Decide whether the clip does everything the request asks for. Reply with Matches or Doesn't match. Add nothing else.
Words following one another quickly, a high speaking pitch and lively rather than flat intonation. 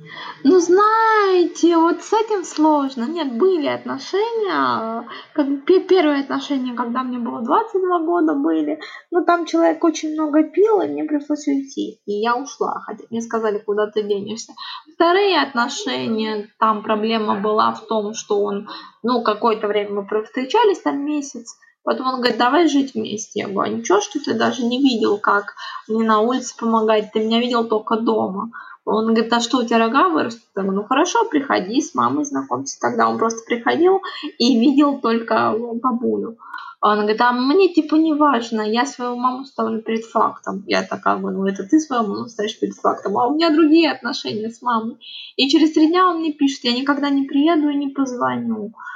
Matches